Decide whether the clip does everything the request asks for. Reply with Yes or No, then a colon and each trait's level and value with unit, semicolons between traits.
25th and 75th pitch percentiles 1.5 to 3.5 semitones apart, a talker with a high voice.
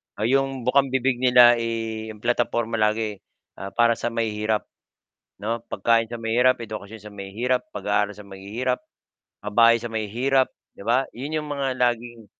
No: narrow, 2.6 semitones; low, 115 Hz